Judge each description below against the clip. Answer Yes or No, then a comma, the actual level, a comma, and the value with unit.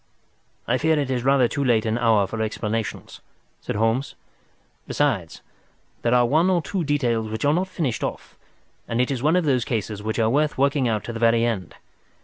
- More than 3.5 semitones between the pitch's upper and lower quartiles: Yes, average, 4.1 semitones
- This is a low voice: Yes, low, 120 Hz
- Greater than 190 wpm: Yes, average, 200 wpm